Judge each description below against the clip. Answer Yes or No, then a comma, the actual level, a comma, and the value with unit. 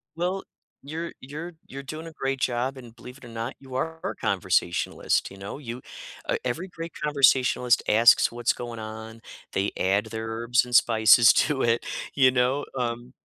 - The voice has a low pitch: Yes, low, 125 Hz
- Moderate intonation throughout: Yes, average, 3.4 semitones